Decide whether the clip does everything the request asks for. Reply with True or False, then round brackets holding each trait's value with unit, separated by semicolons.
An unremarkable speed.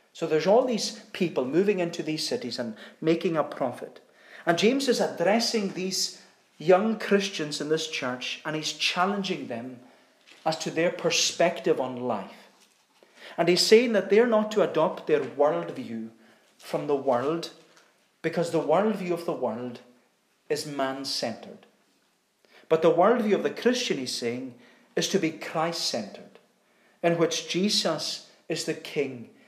True (150 wpm)